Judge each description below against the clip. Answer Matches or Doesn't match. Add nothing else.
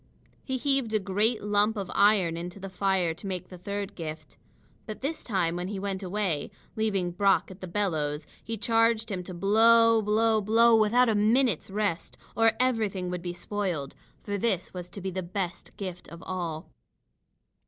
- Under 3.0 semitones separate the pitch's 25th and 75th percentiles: Doesn't match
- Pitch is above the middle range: Matches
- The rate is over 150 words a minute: Matches